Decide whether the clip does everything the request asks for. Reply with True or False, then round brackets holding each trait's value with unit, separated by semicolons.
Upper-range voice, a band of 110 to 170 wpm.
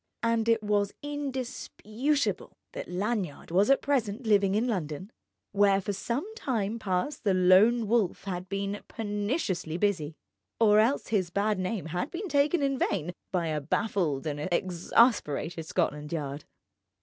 True (205 Hz; 145 wpm)